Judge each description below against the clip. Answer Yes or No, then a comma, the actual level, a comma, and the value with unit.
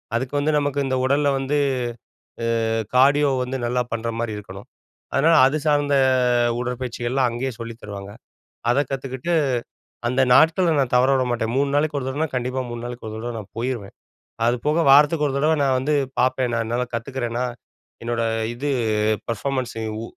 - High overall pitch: No, low, 130 Hz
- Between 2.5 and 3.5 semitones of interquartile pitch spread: Yes, average, 3.0 semitones